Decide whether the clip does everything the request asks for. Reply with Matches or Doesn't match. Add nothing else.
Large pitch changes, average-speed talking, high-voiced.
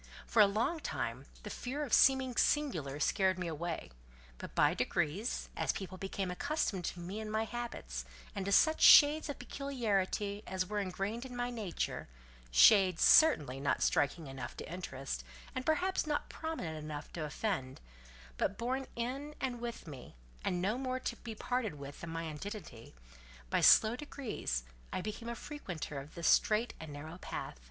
Matches